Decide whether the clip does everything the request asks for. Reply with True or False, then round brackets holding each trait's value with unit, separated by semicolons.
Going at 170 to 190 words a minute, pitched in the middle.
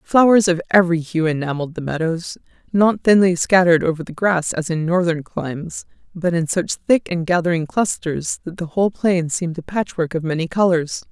True (185 wpm; 170 Hz)